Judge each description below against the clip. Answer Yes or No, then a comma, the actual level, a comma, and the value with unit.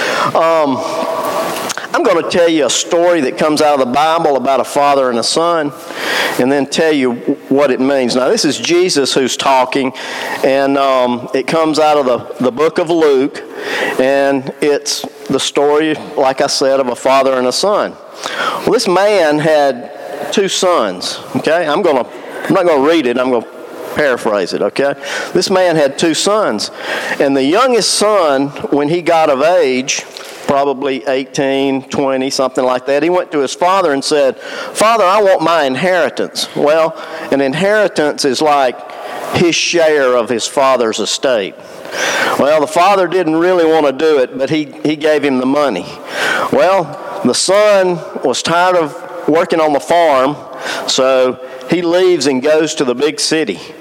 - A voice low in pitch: No, medium, 150 Hz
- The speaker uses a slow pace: No, average, 175 wpm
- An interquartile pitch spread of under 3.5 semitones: No, average, 4.2 semitones